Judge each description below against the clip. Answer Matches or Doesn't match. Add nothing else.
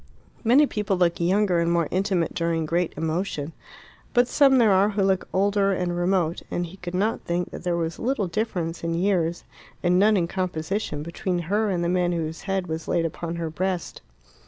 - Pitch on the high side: Doesn't match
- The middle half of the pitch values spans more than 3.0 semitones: Doesn't match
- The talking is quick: Doesn't match